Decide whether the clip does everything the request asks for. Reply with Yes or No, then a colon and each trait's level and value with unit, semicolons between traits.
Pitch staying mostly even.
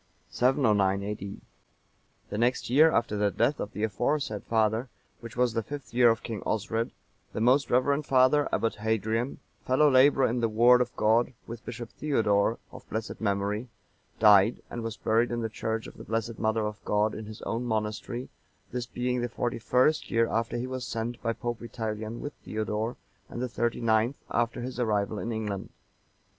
Yes: narrow, 2.2 semitones